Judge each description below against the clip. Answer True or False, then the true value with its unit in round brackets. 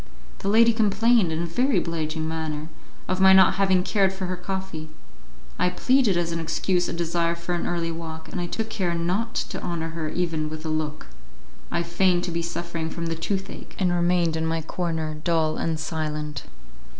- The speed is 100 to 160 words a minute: False (195 wpm)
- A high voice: False (170 Hz)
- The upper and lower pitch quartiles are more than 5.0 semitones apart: False (2.6 semitones)